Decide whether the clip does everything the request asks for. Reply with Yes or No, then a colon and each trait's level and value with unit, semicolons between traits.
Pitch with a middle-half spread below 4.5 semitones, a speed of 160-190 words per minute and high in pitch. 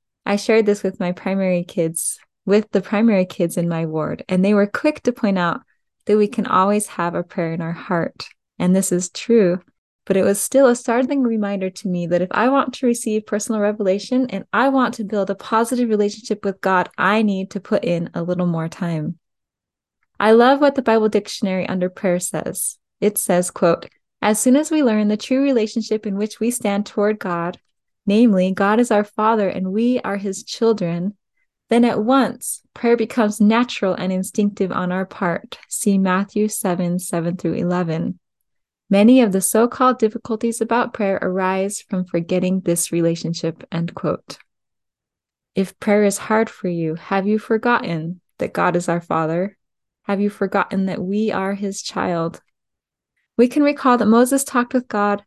Yes: average, 3.6 semitones; average, 185 wpm; high, 200 Hz